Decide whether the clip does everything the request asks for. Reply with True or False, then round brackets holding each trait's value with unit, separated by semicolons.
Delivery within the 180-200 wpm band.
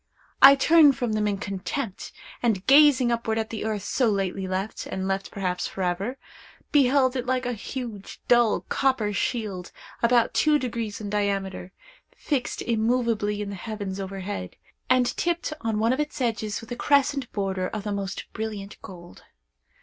False (165 wpm)